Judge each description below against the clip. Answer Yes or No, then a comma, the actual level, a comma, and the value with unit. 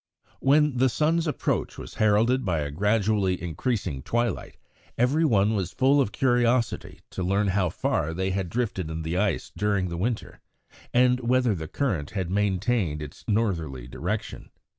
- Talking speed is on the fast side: No, average, 160 wpm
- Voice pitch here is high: No, low, 105 Hz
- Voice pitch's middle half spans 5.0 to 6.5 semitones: Yes, wide, 5.5 semitones